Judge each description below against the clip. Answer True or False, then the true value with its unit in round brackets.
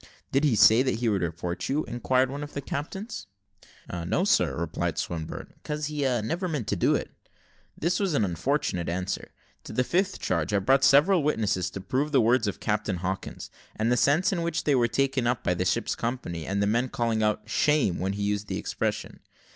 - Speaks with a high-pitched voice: False (120 Hz)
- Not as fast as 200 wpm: False (205 wpm)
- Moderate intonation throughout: False (6.8 semitones)